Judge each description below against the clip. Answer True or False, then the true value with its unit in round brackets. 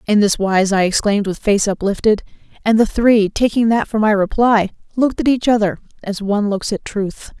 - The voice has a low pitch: False (210 Hz)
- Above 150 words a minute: True (205 wpm)